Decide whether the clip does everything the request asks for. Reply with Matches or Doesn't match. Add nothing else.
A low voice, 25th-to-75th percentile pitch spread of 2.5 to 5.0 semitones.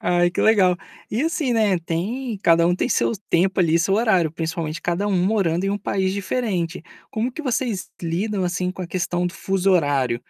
Doesn't match